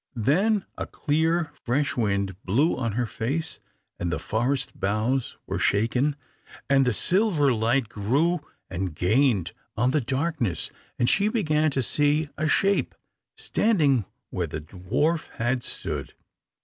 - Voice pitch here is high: No, low, 135 Hz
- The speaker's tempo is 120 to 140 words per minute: Yes, slow, 135 wpm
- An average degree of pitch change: No, wide, 5.9 semitones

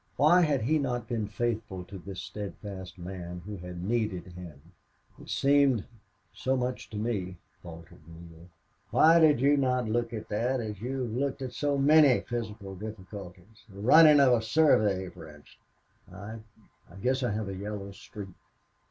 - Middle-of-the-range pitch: No, low, 110 Hz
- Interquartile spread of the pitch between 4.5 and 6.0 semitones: Yes, wide, 5.4 semitones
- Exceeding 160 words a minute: Yes, average, 170 wpm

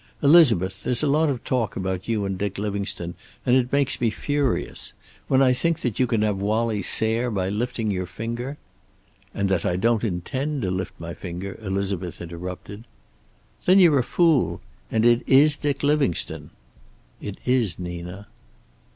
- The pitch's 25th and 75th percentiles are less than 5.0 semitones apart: No, wide, 5.5 semitones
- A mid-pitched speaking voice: No, low, 110 Hz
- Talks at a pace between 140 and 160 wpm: No, average, 170 wpm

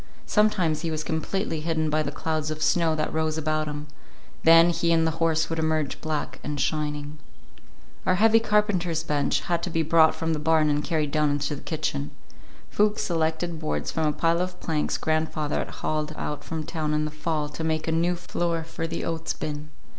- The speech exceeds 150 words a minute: Yes, average, 200 wpm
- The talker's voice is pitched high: No, medium, 160 Hz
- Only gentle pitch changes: Yes, narrow, 1.4 semitones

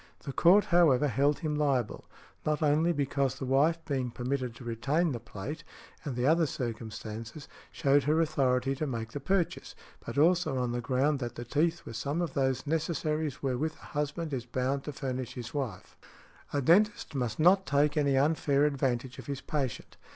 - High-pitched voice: No, medium, 140 Hz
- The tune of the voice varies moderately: Yes, average, 3.4 semitones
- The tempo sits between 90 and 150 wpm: No, average, 180 wpm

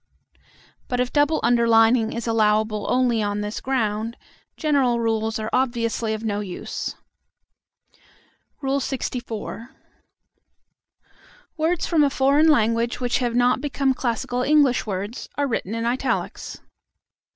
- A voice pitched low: No, high, 235 Hz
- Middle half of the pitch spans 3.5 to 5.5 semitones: No, average, 3.1 semitones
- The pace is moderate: No, slow, 120 wpm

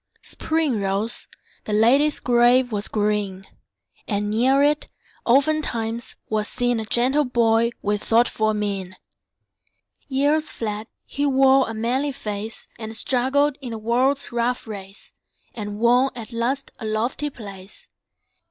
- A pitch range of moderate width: Yes, average, 3.7 semitones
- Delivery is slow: Yes, slow, 130 wpm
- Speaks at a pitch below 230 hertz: No, high, 235 Hz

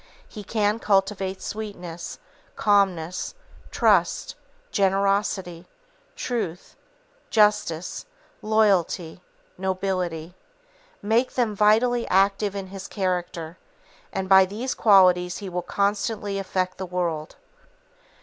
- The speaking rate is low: Yes, slow, 90 wpm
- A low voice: No, high, 195 Hz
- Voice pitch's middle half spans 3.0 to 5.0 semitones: No, narrow, 2.5 semitones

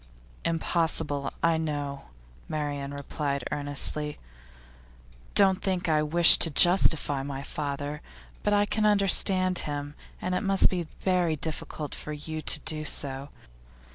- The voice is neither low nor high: Yes, medium, 155 Hz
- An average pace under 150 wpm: Yes, slow, 135 wpm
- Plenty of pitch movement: No, average, 3.7 semitones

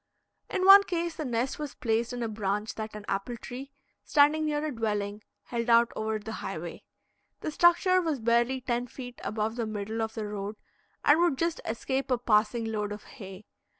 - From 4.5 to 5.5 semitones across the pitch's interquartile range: Yes, average, 4.8 semitones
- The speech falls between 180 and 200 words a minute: Yes, average, 190 wpm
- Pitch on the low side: No, high, 235 Hz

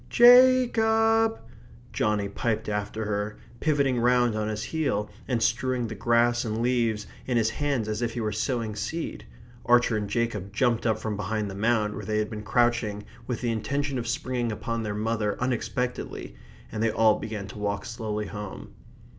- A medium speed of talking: Yes, average, 180 wpm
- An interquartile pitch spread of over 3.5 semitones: No, narrow, 2.6 semitones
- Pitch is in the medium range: No, low, 115 Hz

